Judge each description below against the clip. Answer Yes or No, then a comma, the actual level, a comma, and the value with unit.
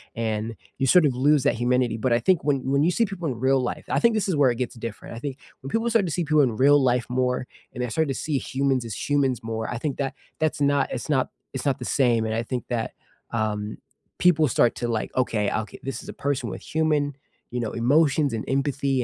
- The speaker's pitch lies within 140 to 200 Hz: No, low, 130 Hz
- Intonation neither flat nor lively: Yes, average, 3.6 semitones